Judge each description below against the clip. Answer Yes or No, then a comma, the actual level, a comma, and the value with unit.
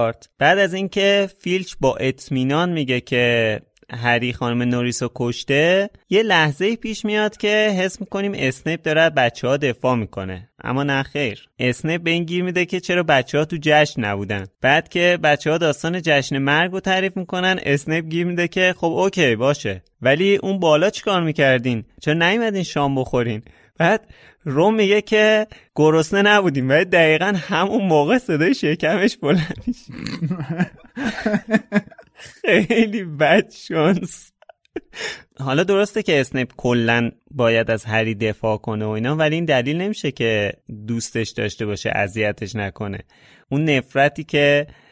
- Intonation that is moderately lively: No, wide, 7.3 semitones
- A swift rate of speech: No, average, 145 wpm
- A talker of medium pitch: Yes, medium, 155 Hz